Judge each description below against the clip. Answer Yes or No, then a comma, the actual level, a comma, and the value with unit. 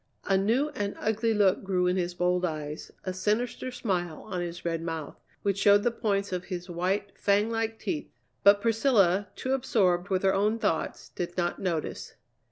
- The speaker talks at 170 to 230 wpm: Yes, average, 180 wpm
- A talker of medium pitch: No, high, 195 Hz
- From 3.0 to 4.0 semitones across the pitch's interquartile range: Yes, average, 3.3 semitones